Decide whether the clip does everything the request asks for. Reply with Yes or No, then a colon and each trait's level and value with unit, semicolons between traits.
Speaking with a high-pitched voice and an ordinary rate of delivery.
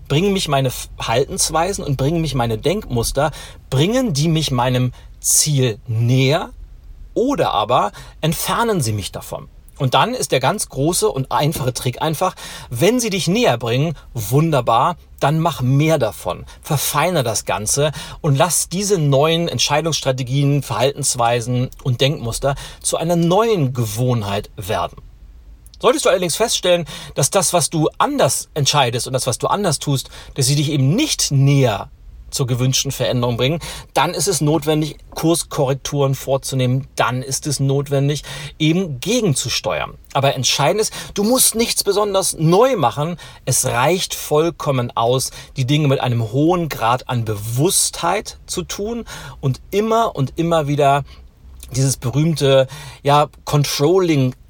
No: medium, 140 Hz; average, 140 wpm